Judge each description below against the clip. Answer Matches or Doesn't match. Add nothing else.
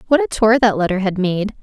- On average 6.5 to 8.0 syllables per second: Doesn't match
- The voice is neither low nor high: Doesn't match